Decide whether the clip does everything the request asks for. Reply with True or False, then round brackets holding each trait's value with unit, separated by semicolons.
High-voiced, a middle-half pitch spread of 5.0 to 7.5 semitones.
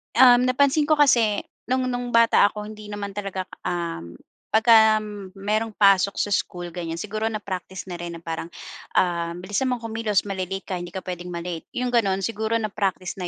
False (205 Hz; 4.0 semitones)